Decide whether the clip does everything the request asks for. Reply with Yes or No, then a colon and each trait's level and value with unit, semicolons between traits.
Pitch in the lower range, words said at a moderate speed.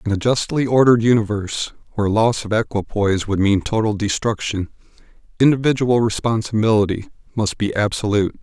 No: low, 110 Hz; slow, 130 wpm